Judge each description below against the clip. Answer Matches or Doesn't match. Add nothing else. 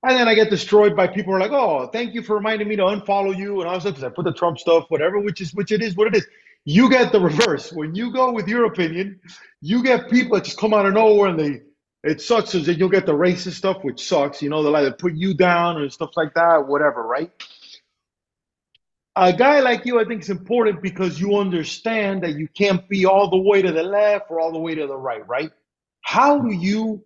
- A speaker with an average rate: Doesn't match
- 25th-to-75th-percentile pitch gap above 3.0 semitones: Matches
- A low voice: Doesn't match